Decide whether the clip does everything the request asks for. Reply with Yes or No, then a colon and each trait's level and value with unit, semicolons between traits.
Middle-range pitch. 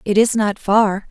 No: high, 210 Hz